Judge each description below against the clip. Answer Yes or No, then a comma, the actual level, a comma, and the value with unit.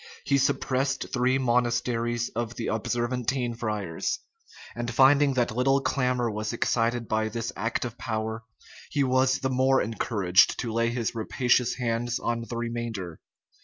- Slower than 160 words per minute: Yes, average, 145 wpm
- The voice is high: No, low, 120 Hz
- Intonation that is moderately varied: No, narrow, 2.0 semitones